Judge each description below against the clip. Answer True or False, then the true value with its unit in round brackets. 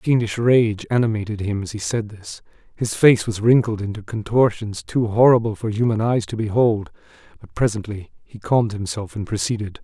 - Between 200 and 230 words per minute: False (175 wpm)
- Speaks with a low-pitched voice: True (110 Hz)